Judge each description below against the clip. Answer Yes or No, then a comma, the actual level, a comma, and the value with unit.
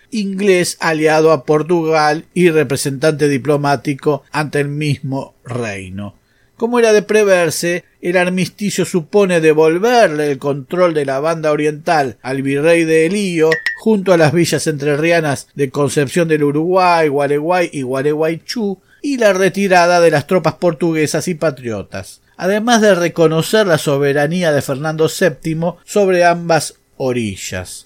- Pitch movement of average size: Yes, average, 3.8 semitones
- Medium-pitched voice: Yes, medium, 160 Hz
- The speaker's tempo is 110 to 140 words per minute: Yes, average, 130 wpm